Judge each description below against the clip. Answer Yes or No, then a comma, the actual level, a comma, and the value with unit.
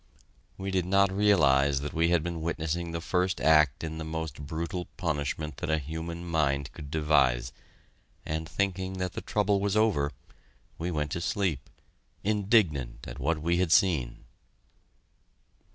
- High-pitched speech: No, very low, 80 Hz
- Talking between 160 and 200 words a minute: No, average, 150 wpm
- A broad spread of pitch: No, average, 3.7 semitones